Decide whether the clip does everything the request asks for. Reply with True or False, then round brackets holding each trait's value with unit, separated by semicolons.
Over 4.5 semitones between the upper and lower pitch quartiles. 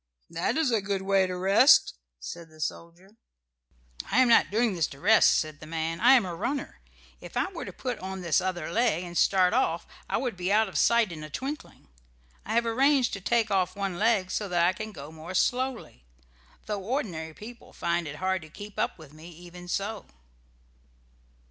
True (5.0 semitones)